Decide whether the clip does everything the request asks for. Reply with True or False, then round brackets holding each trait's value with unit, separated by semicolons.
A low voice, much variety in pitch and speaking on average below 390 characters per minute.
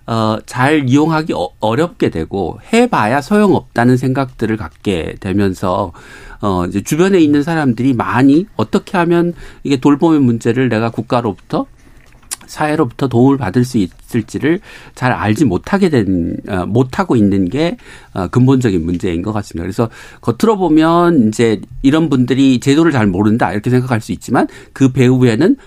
True (125 Hz; 5.8 semitones; 330 characters per minute)